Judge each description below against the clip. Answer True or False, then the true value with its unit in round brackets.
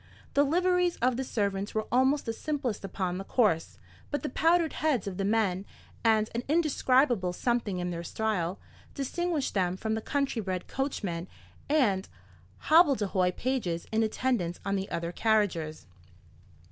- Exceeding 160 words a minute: False (150 wpm)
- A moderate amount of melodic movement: False (6.3 semitones)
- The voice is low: False (220 Hz)